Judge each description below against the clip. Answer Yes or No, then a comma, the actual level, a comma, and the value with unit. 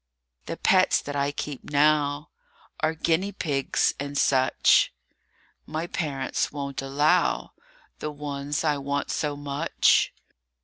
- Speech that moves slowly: Yes, slow, 120 wpm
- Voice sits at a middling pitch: Yes, medium, 145 Hz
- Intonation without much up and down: Yes, narrow, 1.4 semitones